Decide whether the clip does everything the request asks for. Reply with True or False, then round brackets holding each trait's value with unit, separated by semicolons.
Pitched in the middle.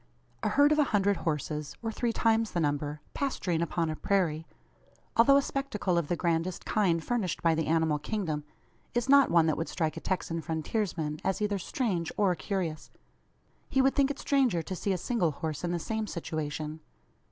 True (175 Hz)